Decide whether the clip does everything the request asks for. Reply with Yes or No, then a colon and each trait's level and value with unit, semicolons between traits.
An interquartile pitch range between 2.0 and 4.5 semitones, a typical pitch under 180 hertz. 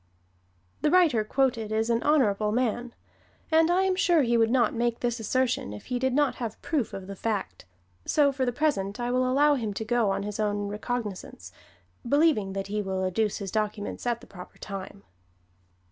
No: average, 4.1 semitones; high, 230 Hz